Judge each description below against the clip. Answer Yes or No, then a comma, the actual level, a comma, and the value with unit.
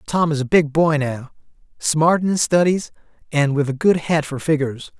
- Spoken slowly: No, fast, 205 wpm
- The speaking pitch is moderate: Yes, medium, 150 Hz